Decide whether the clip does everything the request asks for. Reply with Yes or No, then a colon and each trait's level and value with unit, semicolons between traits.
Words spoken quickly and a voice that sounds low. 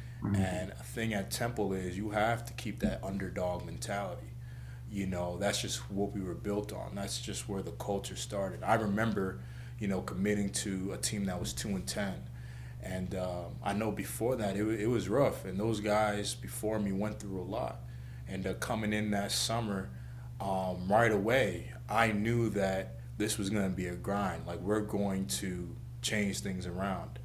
No: average, 190 wpm; low, 100 Hz